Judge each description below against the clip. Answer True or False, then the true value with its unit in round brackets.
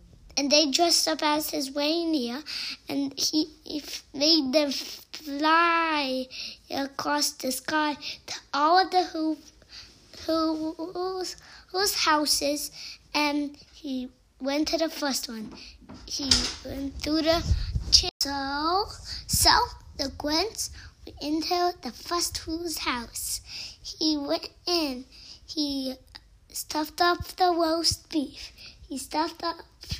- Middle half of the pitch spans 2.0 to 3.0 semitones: True (2.7 semitones)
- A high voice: True (310 Hz)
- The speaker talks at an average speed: False (120 wpm)